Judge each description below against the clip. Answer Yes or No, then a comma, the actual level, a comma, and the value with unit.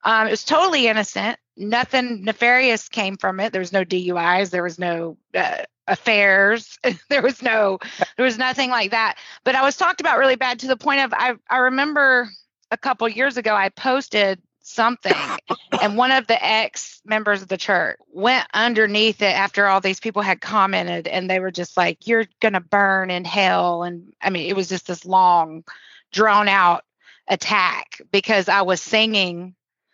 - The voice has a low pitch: No, high, 210 Hz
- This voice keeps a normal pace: Yes, average, 180 wpm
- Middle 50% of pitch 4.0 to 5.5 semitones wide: Yes, average, 4.5 semitones